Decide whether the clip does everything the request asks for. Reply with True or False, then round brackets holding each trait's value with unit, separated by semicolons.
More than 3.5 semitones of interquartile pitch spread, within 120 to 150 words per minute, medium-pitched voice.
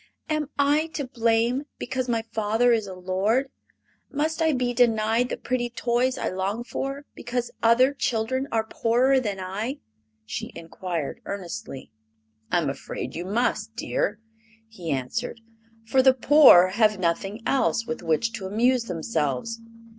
False (4.7 semitones; 145 wpm; 230 Hz)